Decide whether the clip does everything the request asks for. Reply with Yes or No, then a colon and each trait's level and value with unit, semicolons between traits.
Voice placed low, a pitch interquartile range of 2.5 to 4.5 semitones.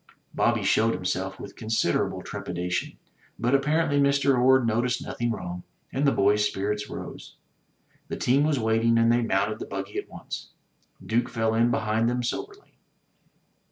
Yes: low, 115 Hz; average, 3.4 semitones